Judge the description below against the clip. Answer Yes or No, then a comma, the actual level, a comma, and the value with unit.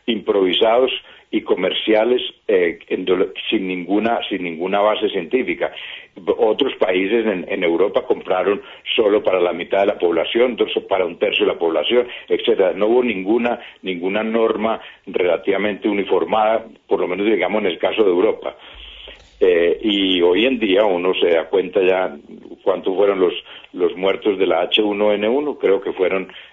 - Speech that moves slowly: No, average, 150 wpm